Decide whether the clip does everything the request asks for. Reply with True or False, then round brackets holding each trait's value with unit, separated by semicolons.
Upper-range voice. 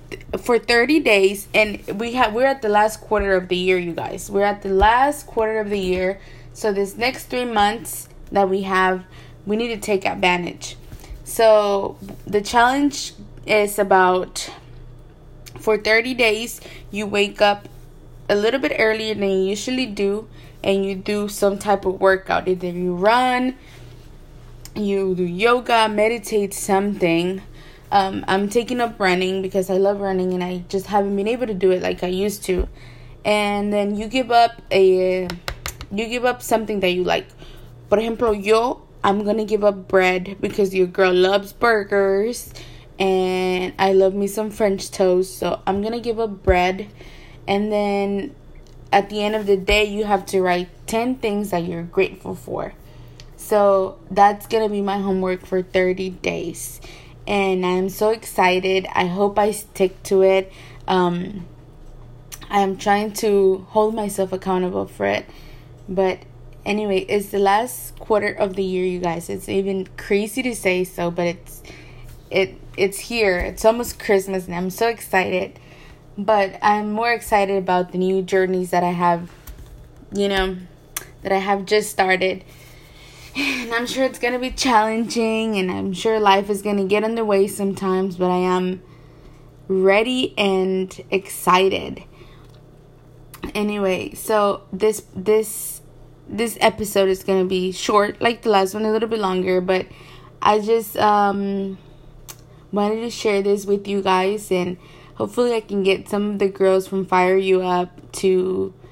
True (195 Hz)